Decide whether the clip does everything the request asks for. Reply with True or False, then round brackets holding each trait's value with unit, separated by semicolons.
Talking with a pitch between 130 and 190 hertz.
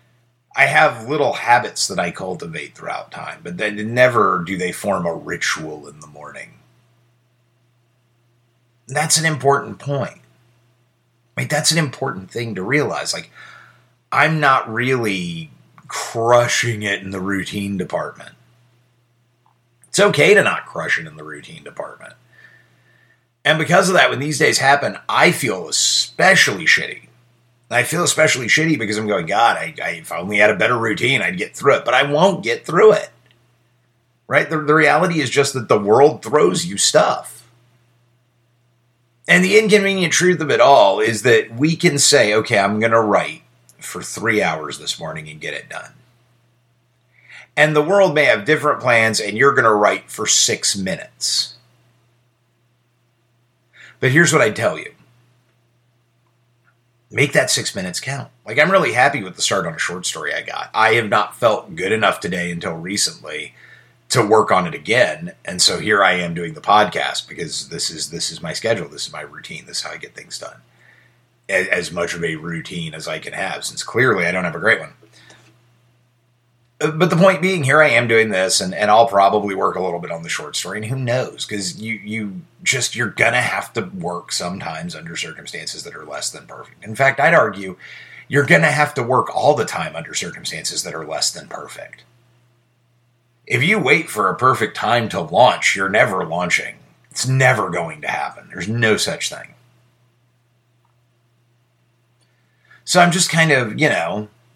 False (120 Hz)